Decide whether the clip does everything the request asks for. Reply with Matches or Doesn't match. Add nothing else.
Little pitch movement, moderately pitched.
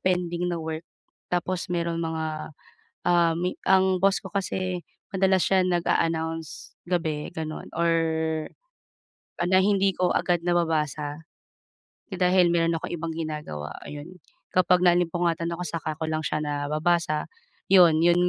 Matches